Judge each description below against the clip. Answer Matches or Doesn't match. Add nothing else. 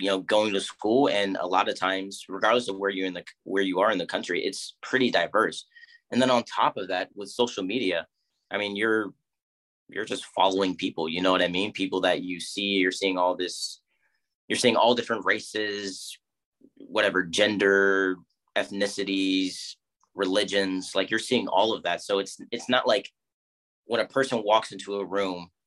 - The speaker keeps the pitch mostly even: Matches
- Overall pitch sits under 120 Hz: Matches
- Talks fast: Doesn't match